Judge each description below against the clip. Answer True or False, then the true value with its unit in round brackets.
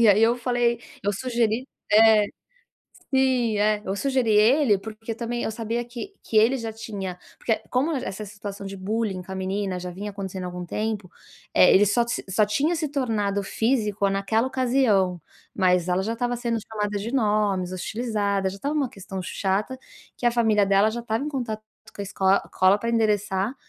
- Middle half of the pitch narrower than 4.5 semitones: True (3.2 semitones)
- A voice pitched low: False (215 Hz)